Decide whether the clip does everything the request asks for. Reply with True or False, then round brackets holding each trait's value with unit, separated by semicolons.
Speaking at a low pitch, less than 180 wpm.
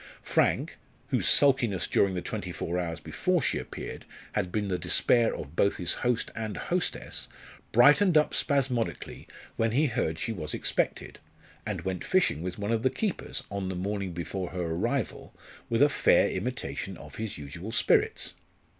True (105 Hz; 165 wpm)